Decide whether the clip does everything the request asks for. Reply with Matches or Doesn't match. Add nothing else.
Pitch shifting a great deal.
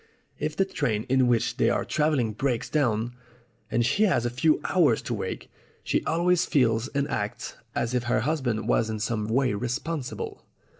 Doesn't match